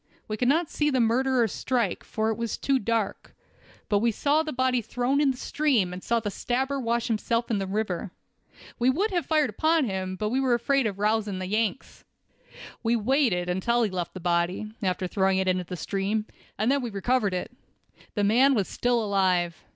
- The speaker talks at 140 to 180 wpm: No, average, 200 wpm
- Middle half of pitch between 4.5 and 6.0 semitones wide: Yes, average, 4.9 semitones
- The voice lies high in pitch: Yes, high, 225 Hz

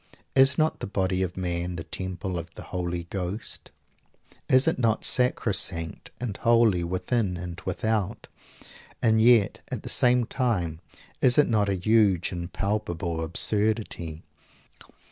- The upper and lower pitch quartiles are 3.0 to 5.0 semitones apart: Yes, average, 4.5 semitones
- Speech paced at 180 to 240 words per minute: No, average, 140 wpm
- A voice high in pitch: No, very low, 95 Hz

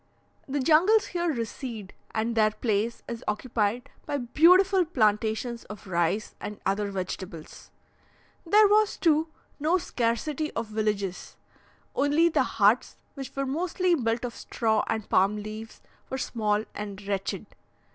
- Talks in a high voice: Yes, high, 230 Hz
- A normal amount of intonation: No, wide, 6.5 semitones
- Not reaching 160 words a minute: Yes, slow, 135 wpm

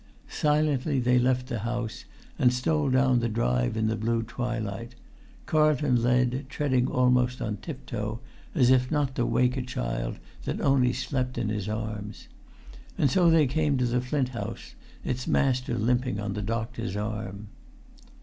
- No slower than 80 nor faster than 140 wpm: No, average, 160 wpm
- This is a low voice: Yes, low, 125 Hz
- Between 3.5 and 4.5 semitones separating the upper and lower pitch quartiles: No, average, 2.8 semitones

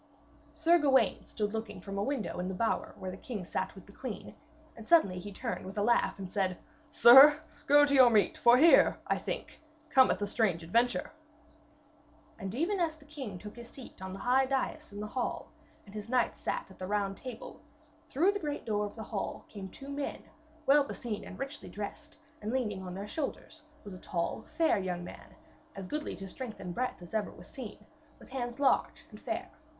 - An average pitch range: No, wide, 5.7 semitones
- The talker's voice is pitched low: No, high, 225 Hz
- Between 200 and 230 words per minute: Yes, fast, 205 wpm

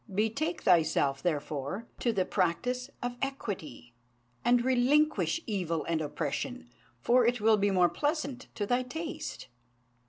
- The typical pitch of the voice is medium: No, high, 225 Hz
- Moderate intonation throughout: No, wide, 6.5 semitones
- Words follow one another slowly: Yes, slow, 130 wpm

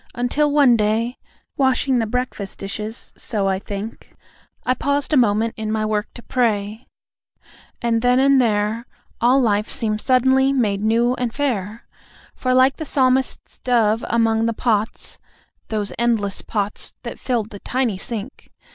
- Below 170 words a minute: Yes, average, 150 wpm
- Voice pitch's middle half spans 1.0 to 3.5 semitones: Yes, average, 3.1 semitones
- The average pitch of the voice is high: Yes, high, 230 Hz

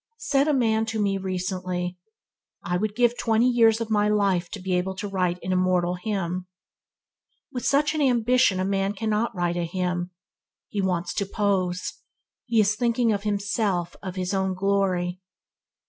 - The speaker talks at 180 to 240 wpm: No, average, 170 wpm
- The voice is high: Yes, high, 195 Hz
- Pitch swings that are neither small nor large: Yes, average, 3.3 semitones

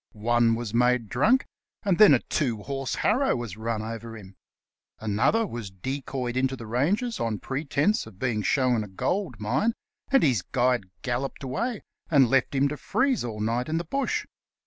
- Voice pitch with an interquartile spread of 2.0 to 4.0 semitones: No, average, 4.7 semitones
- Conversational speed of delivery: Yes, average, 175 wpm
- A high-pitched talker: No, low, 125 Hz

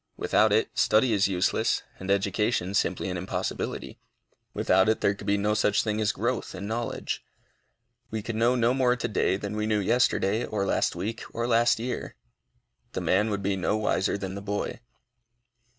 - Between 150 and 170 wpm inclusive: No, average, 180 wpm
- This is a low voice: Yes, low, 105 Hz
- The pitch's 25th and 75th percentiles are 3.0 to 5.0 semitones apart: No, narrow, 2.5 semitones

